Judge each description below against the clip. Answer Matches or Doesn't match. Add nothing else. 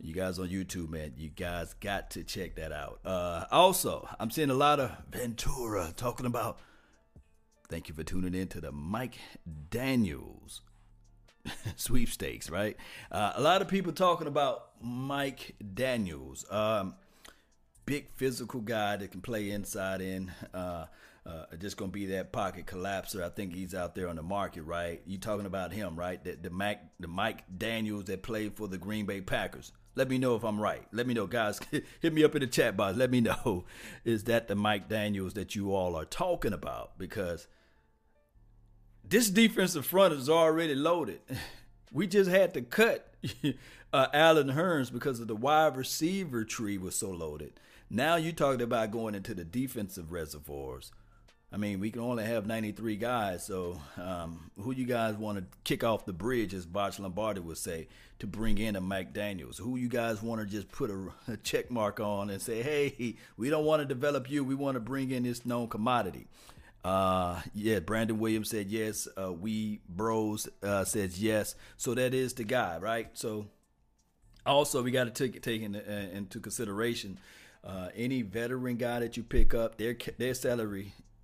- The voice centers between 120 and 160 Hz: Doesn't match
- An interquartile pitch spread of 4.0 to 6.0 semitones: Matches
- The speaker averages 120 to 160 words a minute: Doesn't match